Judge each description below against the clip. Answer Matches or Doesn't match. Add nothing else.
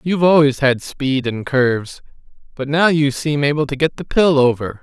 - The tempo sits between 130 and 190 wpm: Doesn't match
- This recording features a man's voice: Matches